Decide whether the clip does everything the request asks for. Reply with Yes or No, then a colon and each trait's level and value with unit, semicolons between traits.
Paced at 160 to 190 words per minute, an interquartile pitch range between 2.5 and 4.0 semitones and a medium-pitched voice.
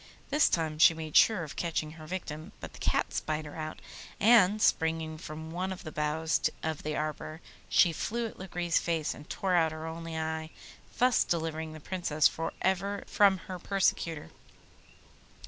Yes: average, 175 wpm; average, 2.8 semitones; medium, 160 Hz